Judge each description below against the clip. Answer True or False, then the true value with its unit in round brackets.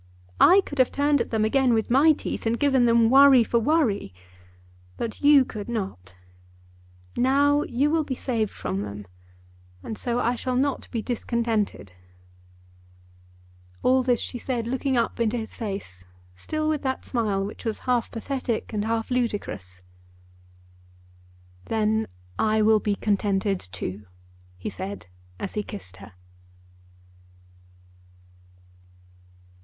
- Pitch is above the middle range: True (230 Hz)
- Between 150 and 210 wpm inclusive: False (135 wpm)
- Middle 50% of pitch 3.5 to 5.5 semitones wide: True (4.2 semitones)